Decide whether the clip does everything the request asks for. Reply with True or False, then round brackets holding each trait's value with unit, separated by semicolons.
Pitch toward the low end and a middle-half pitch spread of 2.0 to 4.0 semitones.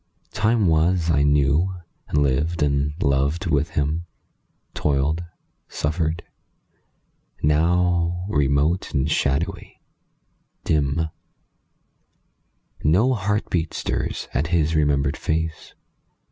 True (80 Hz; 3.0 semitones)